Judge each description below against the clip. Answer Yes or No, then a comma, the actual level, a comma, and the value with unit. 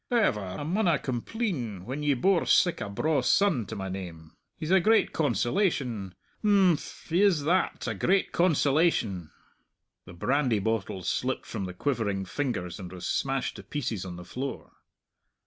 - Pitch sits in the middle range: No, low, 130 Hz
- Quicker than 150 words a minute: Yes, average, 160 wpm